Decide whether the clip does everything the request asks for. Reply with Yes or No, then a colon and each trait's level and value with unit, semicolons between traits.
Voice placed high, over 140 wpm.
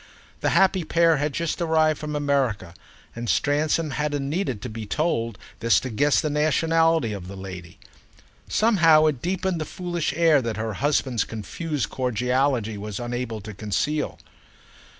No: medium, 140 Hz; average, 150 wpm